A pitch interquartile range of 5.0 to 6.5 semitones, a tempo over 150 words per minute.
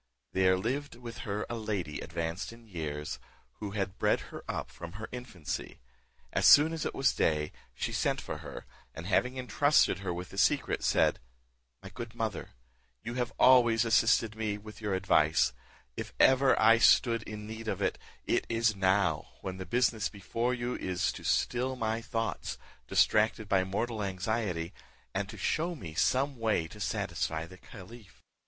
No: average, 4.1 semitones; average, 175 wpm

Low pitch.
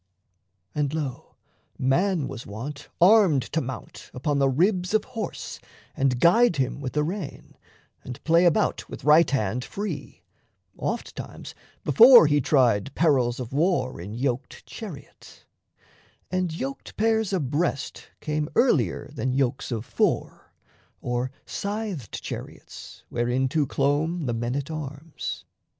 No: medium, 145 Hz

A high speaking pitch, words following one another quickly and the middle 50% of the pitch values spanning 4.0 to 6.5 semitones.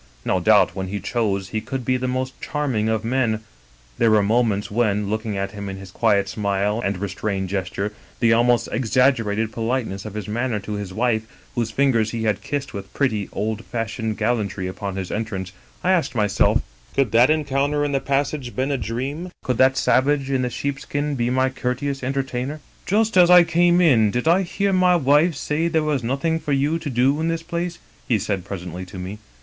No: low, 120 Hz; fast, 210 wpm; average, 5.2 semitones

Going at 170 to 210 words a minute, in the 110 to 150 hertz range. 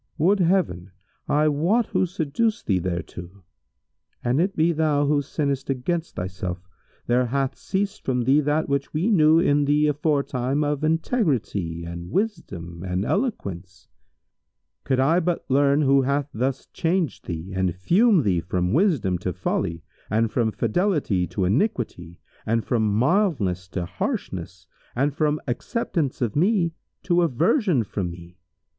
No: average, 145 wpm; medium, 140 Hz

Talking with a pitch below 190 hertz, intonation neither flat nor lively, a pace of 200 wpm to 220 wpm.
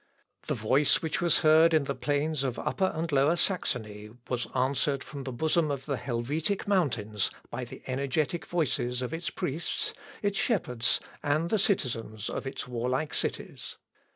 No: medium, 140 Hz; average, 4.6 semitones; average, 160 wpm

